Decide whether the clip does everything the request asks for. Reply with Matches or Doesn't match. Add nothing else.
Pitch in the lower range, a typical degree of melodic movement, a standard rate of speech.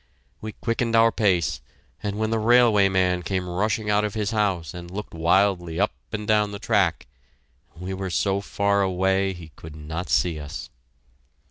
Matches